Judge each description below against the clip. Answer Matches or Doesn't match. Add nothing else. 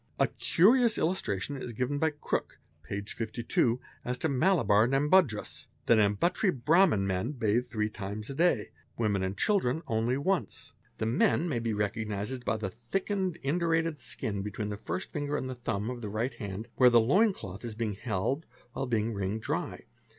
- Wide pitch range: Matches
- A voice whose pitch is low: Matches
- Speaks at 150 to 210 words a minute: Matches